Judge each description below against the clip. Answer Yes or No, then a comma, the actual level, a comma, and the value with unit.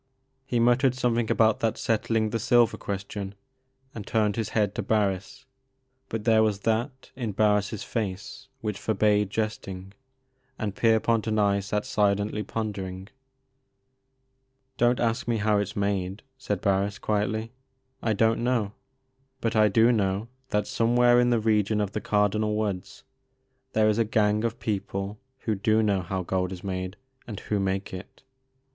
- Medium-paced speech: Yes, average, 160 wpm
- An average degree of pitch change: No, narrow, 2.1 semitones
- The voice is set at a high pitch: No, low, 105 Hz